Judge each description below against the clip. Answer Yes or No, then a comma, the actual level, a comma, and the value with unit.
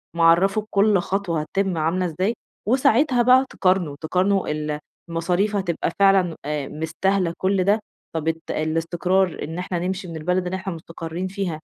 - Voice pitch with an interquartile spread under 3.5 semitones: Yes, average, 3.1 semitones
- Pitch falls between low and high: Yes, medium, 180 Hz